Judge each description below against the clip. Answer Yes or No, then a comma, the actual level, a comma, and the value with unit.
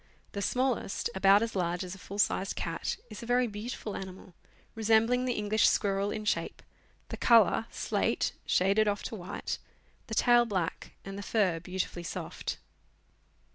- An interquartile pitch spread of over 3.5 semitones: No, average, 3.0 semitones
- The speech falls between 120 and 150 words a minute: No, average, 160 wpm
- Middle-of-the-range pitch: No, high, 205 Hz